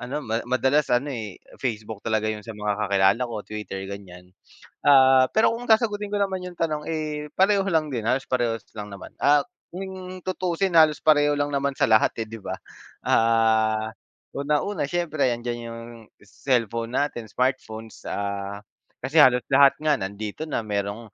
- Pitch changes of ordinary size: No, wide, 5.8 semitones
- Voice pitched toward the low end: Yes, low, 130 Hz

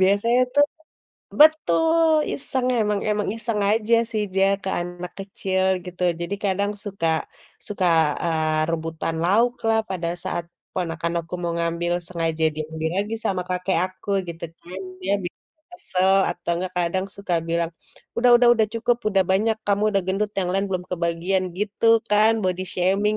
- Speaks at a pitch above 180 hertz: Yes, high, 190 Hz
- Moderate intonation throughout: Yes, average, 3.4 semitones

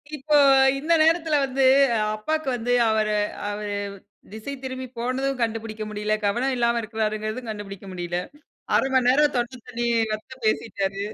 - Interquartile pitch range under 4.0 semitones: Yes, average, 3.6 semitones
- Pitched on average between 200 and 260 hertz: Yes, high, 235 Hz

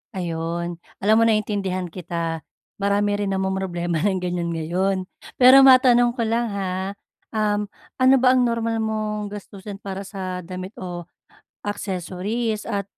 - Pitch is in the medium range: No, high, 200 Hz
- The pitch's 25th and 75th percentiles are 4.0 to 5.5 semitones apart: No, average, 3.1 semitones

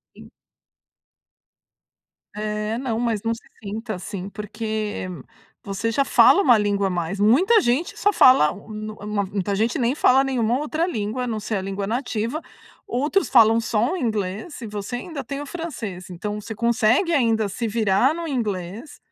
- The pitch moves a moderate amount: Yes, average, 3.8 semitones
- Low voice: No, high, 225 Hz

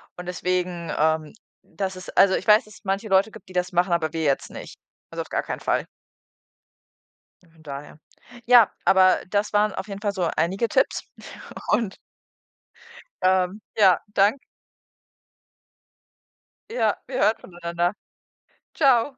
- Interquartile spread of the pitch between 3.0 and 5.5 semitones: Yes, average, 3.3 semitones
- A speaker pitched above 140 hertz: Yes, high, 190 Hz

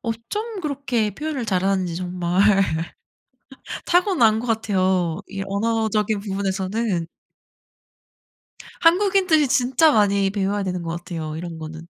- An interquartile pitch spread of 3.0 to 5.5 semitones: Yes, average, 5.2 semitones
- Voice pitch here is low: No, high, 205 Hz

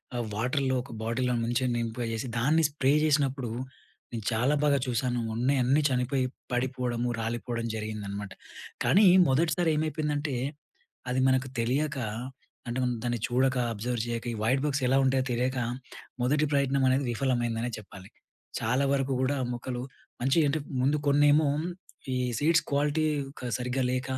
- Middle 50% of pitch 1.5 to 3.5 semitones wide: Yes, average, 2.9 semitones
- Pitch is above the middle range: No, low, 130 Hz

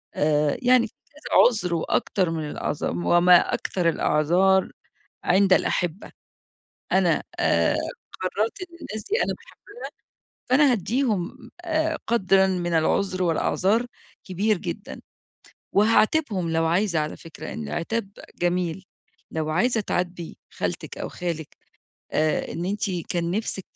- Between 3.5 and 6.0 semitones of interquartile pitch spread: Yes, average, 4.5 semitones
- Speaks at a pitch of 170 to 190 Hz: Yes, medium, 185 Hz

